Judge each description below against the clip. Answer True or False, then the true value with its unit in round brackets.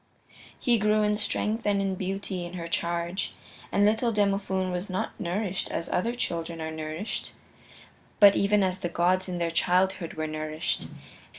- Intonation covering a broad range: False (3.1 semitones)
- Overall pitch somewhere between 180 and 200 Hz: True (185 Hz)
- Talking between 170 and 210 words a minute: False (160 wpm)